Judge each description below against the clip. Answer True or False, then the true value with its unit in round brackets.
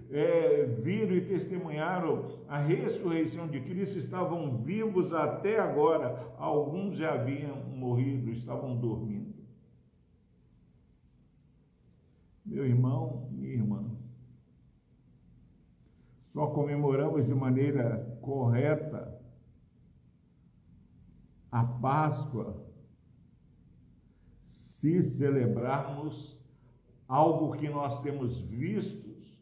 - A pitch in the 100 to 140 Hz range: True (135 Hz)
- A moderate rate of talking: False (75 wpm)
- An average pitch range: True (4.3 semitones)